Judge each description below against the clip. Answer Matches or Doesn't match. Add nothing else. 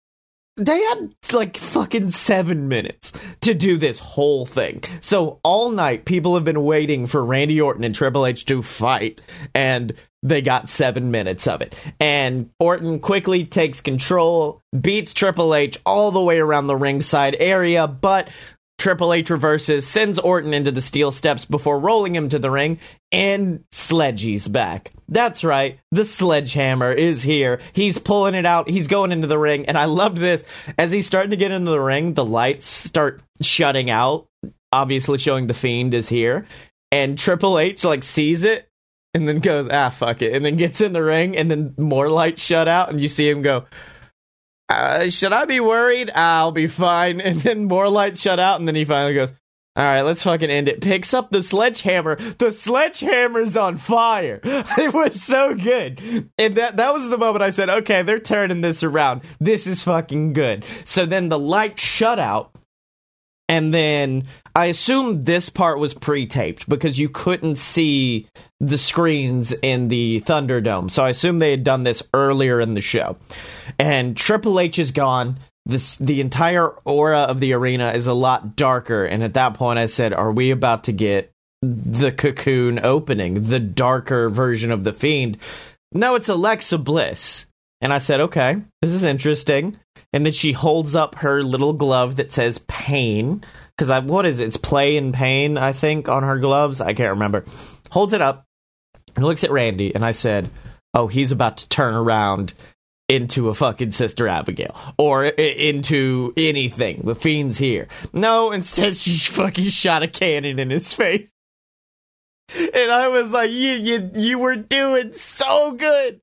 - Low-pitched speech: Doesn't match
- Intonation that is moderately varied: Doesn't match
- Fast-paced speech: Doesn't match